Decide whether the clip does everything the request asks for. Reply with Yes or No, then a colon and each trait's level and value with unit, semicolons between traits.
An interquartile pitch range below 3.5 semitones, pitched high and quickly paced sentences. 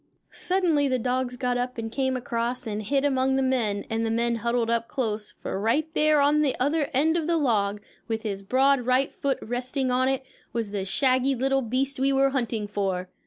Yes: average, 3.1 semitones; very high, 255 Hz; fast, 210 wpm